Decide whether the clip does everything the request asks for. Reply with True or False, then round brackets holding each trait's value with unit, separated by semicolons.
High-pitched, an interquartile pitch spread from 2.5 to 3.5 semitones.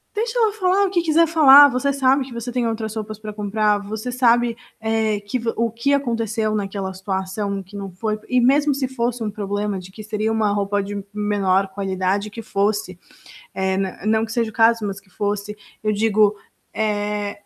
True (215 Hz; 2.9 semitones)